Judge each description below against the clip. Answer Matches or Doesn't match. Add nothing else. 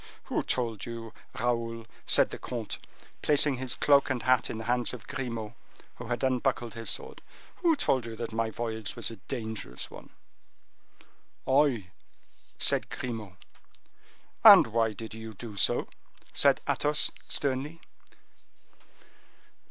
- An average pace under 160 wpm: Matches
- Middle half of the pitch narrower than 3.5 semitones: Matches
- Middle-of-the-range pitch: Doesn't match